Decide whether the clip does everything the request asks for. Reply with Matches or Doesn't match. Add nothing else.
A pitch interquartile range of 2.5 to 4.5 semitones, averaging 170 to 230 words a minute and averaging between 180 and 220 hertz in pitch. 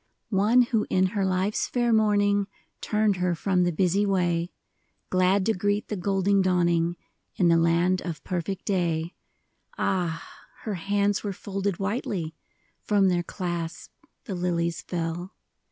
Doesn't match